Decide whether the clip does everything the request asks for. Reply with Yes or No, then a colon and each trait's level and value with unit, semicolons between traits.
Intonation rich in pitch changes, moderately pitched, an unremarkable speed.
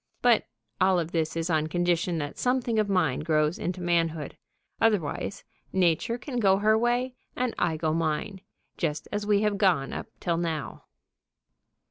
No: average, 4.7 semitones; medium, 175 Hz; average, 160 wpm